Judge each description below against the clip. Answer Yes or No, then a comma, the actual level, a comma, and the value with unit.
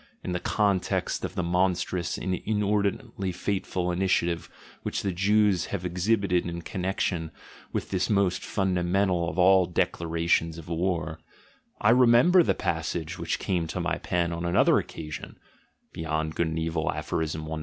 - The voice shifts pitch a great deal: No, narrow, 2.4 semitones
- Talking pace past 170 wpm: No, average, 150 wpm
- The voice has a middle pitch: No, very low, 90 Hz